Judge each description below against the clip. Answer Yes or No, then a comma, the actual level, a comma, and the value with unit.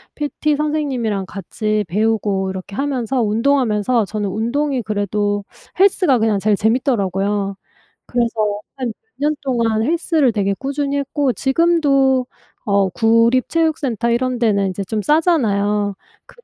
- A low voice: No, high, 230 Hz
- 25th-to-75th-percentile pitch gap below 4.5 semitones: No, average, 5.2 semitones